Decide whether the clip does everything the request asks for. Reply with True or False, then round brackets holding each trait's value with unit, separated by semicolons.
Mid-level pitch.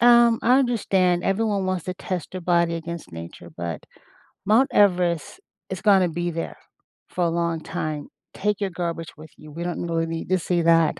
True (175 Hz)